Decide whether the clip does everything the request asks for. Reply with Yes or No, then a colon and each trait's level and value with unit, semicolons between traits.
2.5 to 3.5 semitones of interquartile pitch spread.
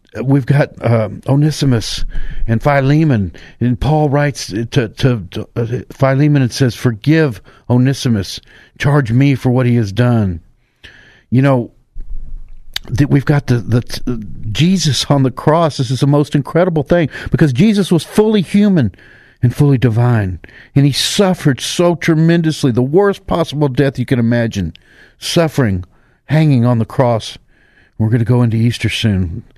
No: average, 4.1 semitones